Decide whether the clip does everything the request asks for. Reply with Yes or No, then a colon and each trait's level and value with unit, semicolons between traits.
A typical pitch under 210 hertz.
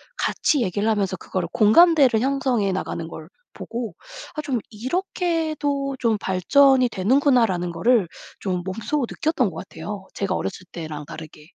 No: high, 225 Hz